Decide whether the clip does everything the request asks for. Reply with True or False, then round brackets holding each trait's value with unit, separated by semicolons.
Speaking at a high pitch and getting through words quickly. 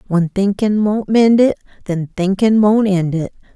False (200 Hz; 170 wpm)